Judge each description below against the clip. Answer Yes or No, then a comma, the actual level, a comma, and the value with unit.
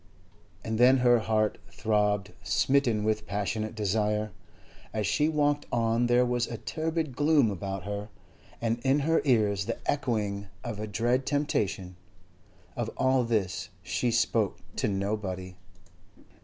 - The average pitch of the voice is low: Yes, low, 110 Hz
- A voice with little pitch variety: No, average, 3.6 semitones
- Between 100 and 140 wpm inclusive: Yes, slow, 135 wpm